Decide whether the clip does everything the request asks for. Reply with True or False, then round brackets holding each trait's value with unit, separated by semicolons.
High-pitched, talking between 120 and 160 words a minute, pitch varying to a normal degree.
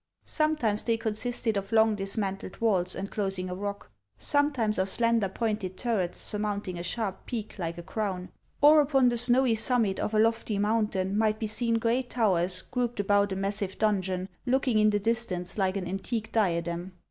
False (210 Hz; 180 wpm; 3.3 semitones)